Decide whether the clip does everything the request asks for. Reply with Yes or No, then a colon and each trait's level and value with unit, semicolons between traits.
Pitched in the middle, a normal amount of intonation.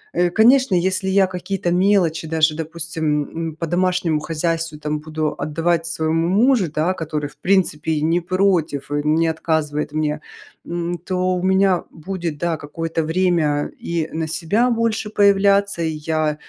Yes: medium, 165 Hz; average, 3.1 semitones